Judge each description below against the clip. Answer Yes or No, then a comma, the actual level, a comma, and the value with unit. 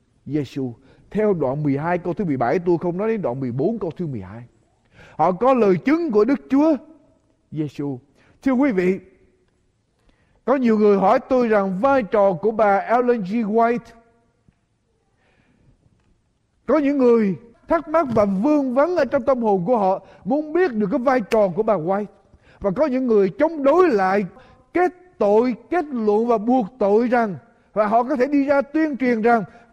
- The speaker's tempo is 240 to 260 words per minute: No, average, 180 wpm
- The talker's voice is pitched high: Yes, high, 220 Hz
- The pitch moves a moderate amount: No, wide, 6.0 semitones